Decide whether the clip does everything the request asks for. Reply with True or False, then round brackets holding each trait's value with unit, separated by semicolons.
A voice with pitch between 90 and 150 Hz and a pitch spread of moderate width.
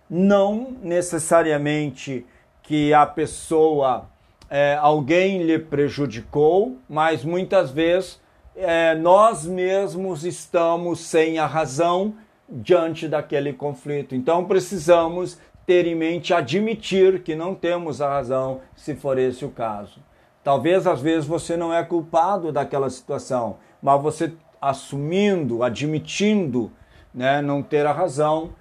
False (160 Hz; 3.6 semitones)